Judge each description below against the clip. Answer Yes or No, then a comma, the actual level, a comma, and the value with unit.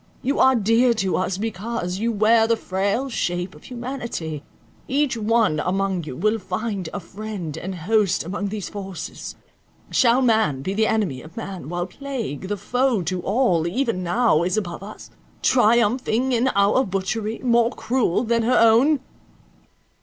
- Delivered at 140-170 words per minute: Yes, average, 160 wpm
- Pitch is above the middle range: Yes, high, 215 Hz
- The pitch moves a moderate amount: Yes, average, 4.3 semitones